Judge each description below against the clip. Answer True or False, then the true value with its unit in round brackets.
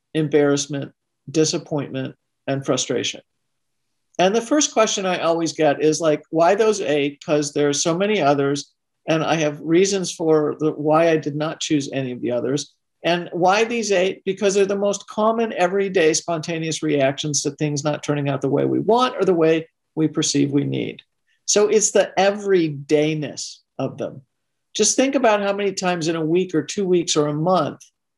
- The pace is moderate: True (185 wpm)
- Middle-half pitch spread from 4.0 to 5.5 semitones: True (4.6 semitones)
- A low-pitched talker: False (155 Hz)